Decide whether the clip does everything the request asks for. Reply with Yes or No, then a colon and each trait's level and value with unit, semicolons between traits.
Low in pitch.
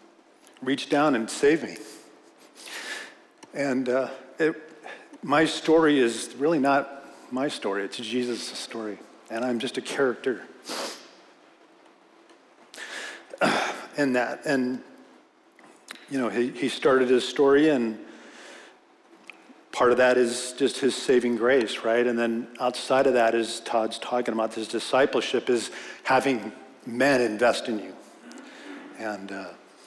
Yes: low, 130 Hz